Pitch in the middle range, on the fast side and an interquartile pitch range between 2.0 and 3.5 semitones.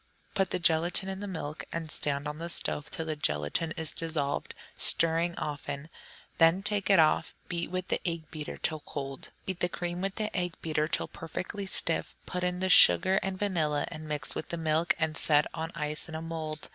Yes: medium, 165 Hz; fast, 210 wpm; average, 2.8 semitones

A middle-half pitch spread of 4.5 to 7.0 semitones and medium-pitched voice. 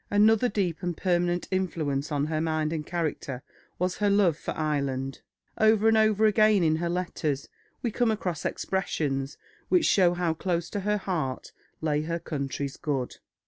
Yes: average, 4.9 semitones; medium, 170 Hz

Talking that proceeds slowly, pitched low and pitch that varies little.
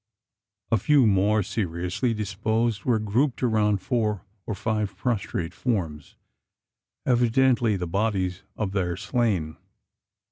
No: slow, 110 wpm; low, 105 Hz; average, 3.7 semitones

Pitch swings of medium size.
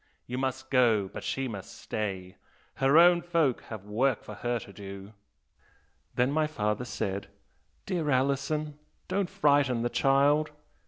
No: wide, 5.8 semitones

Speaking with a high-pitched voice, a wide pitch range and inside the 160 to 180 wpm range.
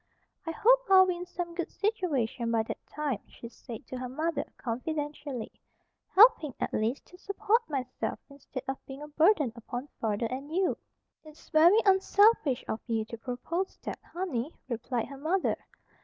Yes: very high, 290 Hz; wide, 6.5 semitones; average, 165 wpm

